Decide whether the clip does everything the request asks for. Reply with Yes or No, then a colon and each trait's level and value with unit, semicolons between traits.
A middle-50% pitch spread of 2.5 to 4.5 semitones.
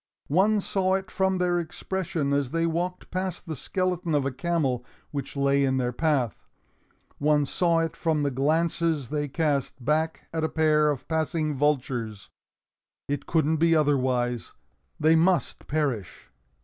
Yes: average, 3.3 semitones